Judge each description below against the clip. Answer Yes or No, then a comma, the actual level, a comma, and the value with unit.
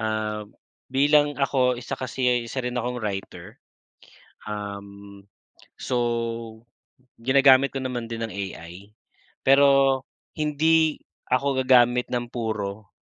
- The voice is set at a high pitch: No, low, 120 Hz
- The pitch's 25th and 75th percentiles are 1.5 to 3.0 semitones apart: No, average, 3.9 semitones